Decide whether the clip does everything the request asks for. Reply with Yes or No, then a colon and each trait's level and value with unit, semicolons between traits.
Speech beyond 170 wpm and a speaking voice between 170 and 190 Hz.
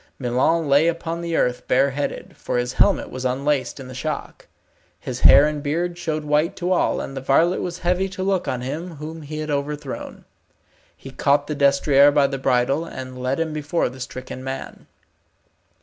No: average, 185 wpm; medium, 145 Hz